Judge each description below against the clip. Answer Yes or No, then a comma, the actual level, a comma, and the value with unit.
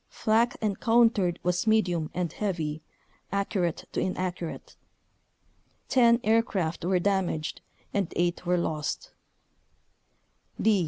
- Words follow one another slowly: Yes, slow, 100 wpm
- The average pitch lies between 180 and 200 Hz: Yes, medium, 185 Hz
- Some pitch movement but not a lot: Yes, average, 4.0 semitones